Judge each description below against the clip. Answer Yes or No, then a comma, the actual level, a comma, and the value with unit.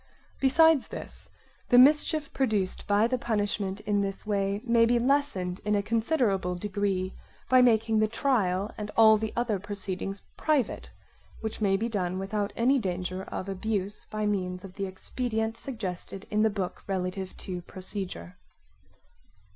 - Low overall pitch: No, high, 205 Hz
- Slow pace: No, average, 150 wpm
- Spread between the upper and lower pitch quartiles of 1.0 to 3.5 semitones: Yes, average, 3.2 semitones